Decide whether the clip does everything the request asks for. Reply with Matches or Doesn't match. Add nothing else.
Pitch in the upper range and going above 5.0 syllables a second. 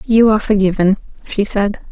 Matches